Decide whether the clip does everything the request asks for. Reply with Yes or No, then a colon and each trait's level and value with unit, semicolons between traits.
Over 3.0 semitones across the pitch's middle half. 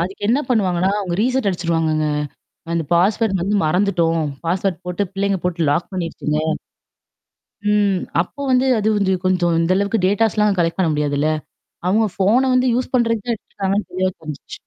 Yes: average, 3.6 semitones